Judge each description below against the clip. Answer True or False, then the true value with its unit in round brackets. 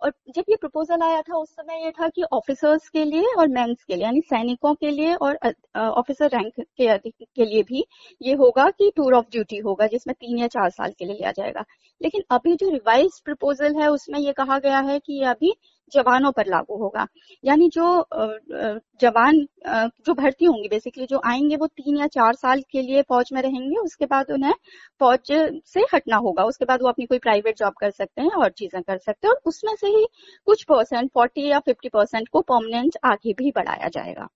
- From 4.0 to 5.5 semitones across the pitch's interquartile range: True (5.1 semitones)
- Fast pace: True (205 wpm)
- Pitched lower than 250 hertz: False (275 Hz)